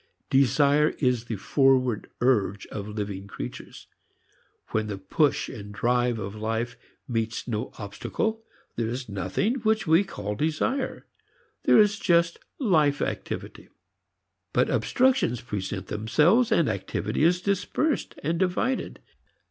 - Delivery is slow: Yes, slow, 125 wpm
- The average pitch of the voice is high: No, low, 125 Hz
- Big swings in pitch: Yes, wide, 8.7 semitones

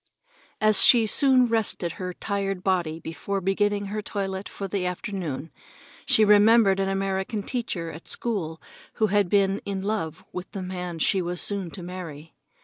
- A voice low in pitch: No, high, 195 Hz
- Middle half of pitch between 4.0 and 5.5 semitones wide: No, narrow, 2.5 semitones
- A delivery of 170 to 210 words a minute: No, average, 155 wpm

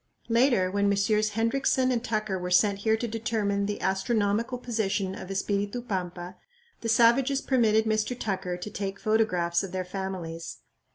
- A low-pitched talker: No, high, 205 Hz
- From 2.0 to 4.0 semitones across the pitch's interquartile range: Yes, average, 3.1 semitones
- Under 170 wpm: Yes, average, 155 wpm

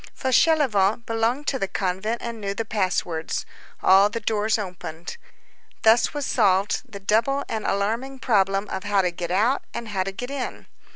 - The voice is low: No, high, 210 Hz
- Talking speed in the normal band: Yes, average, 175 wpm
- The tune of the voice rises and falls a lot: No, average, 3.3 semitones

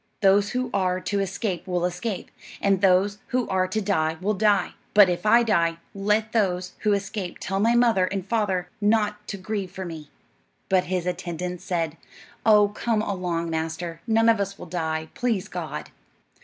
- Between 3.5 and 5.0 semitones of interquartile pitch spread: No, average, 2.7 semitones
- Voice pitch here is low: No, high, 195 Hz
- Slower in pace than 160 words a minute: No, average, 175 wpm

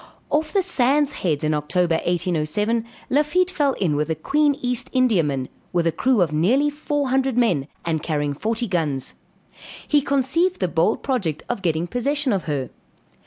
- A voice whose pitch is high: Yes, high, 215 Hz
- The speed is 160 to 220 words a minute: Yes, average, 165 wpm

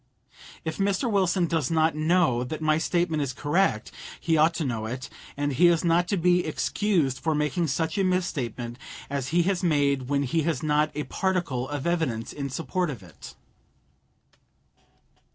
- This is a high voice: No, medium, 155 Hz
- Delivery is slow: No, average, 170 wpm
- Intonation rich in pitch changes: No, average, 4.1 semitones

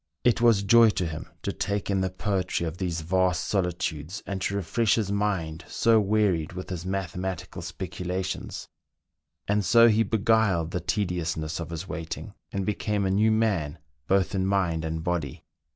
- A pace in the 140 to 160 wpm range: No, average, 195 wpm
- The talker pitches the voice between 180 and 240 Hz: No, very low, 95 Hz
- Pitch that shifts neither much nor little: Yes, average, 3.2 semitones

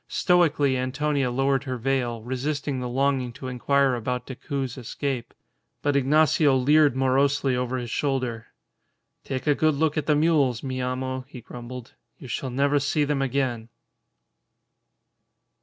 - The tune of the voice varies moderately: No, narrow, 2.1 semitones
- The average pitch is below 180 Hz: Yes, low, 135 Hz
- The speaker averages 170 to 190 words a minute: No, average, 140 wpm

